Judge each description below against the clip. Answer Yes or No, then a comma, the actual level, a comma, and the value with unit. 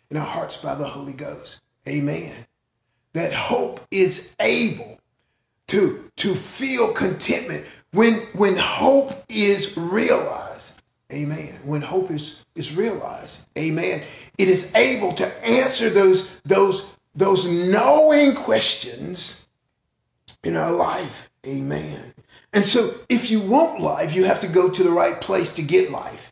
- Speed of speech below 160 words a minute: Yes, slow, 135 wpm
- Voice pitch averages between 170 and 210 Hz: Yes, medium, 185 Hz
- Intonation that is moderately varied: No, wide, 7.1 semitones